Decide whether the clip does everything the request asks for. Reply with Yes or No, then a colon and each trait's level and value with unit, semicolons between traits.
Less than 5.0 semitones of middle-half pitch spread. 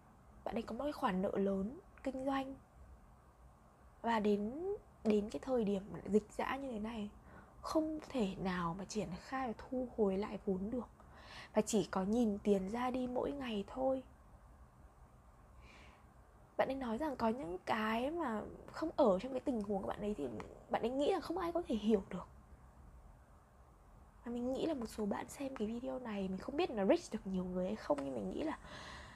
No: average, 5.3 semitones